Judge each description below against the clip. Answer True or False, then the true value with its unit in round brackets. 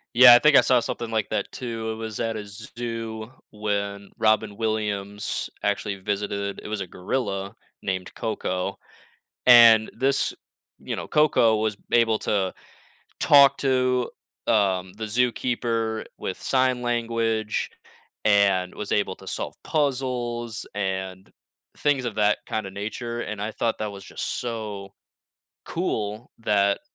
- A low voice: True (110 Hz)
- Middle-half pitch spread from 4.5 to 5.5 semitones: False (2.8 semitones)